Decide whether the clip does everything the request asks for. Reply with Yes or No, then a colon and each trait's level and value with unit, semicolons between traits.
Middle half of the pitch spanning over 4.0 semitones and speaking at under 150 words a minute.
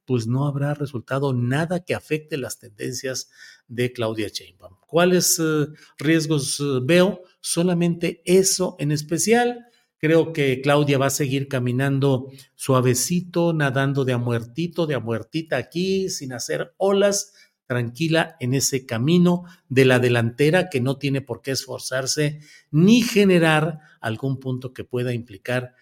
Yes: average, 4.9 semitones; average, 135 wpm